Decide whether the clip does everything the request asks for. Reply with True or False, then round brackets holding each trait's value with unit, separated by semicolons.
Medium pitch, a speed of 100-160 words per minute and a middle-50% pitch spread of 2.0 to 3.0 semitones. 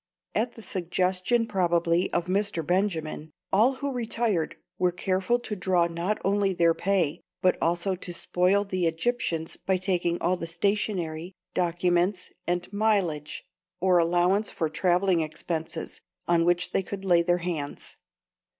True (180 Hz; 140 wpm; 2.6 semitones)